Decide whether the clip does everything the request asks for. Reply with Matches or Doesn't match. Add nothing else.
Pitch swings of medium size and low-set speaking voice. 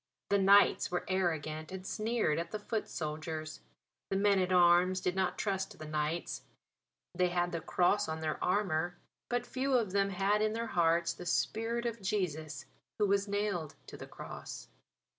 Doesn't match